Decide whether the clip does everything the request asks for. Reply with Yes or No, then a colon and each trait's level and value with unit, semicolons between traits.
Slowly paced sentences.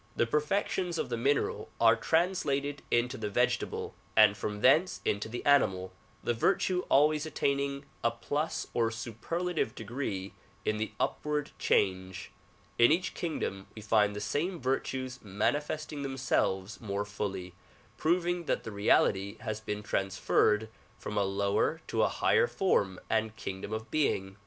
No: average, 150 wpm